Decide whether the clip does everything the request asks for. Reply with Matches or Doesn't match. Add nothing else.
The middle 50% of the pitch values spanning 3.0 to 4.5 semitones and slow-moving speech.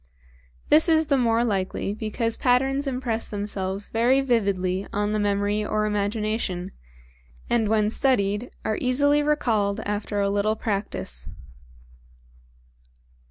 Matches